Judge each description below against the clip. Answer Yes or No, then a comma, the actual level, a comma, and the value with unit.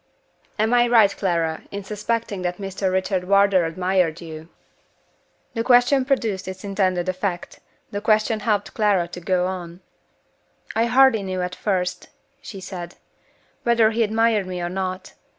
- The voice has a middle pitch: No, high, 195 Hz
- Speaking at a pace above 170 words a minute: No, average, 150 wpm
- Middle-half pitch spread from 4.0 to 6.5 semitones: No, average, 3.3 semitones